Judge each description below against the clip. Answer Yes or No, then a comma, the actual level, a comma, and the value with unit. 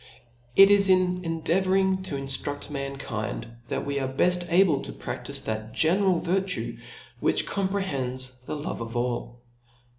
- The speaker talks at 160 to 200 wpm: No, average, 140 wpm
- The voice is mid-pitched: Yes, medium, 160 Hz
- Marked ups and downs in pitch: Yes, wide, 6.4 semitones